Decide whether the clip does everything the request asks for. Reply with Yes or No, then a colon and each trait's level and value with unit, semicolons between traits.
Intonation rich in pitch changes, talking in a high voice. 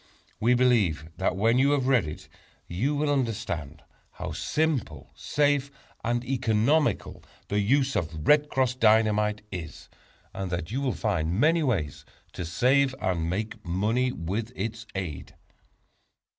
No: wide, 6.4 semitones; low, 110 Hz